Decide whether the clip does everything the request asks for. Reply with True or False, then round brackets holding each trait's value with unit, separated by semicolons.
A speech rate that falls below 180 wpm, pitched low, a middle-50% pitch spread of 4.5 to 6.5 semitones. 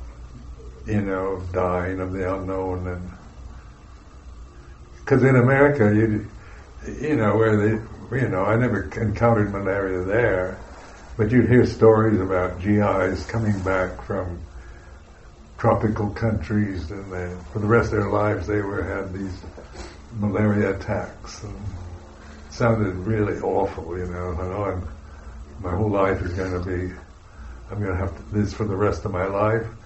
False (145 wpm; 95 Hz; 2.9 semitones)